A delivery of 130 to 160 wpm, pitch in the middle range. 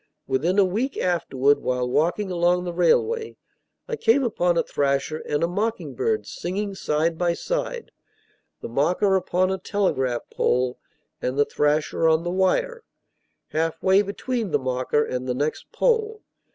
Yes: average, 150 wpm; medium, 175 Hz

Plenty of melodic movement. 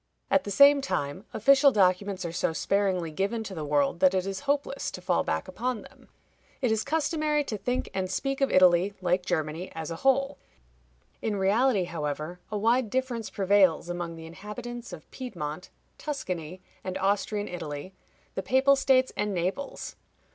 Yes: wide, 6.5 semitones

